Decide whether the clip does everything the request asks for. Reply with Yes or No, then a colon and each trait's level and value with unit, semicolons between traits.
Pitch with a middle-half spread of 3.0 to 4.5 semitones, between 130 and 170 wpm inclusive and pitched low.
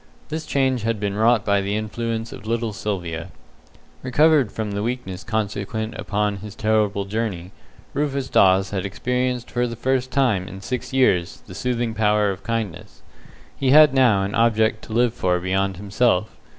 Yes: average, 3.7 semitones; average, 165 wpm; low, 110 Hz